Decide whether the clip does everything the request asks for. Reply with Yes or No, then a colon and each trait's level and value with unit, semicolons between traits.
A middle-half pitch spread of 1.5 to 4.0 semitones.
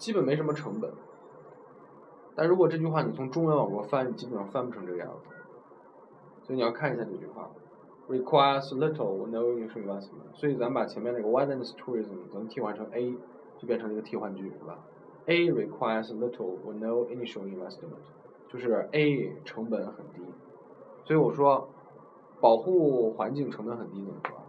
No: average, 5.3 semitones